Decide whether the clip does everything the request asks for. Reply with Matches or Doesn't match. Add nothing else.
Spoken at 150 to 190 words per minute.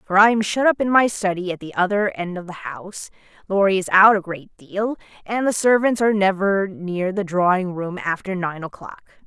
Doesn't match